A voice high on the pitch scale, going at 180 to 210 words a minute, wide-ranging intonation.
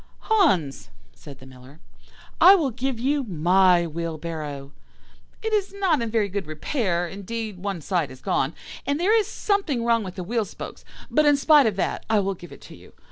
Yes: high, 200 Hz; average, 190 wpm; wide, 9.0 semitones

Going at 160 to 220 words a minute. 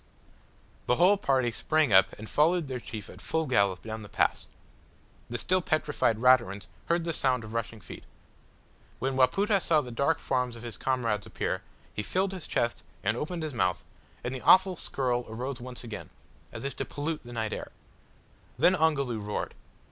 Yes: average, 180 wpm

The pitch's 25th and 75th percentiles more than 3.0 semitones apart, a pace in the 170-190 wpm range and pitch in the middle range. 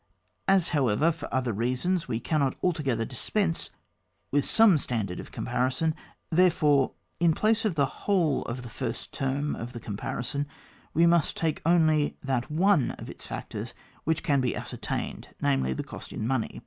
Yes: average, 5.1 semitones; average, 175 wpm; medium, 145 Hz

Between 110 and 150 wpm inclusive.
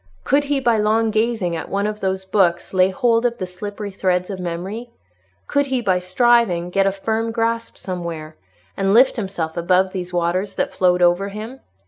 No: average, 185 wpm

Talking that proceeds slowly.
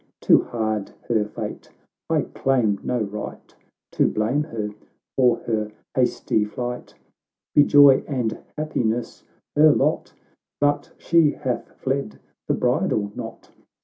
Yes: slow, 125 wpm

